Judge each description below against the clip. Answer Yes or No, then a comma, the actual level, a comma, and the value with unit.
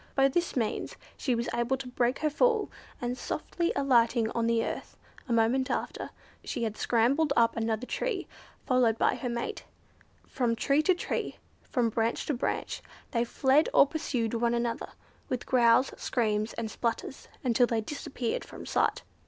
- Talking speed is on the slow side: No, average, 165 wpm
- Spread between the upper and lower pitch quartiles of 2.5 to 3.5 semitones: Yes, average, 2.8 semitones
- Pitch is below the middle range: No, high, 240 Hz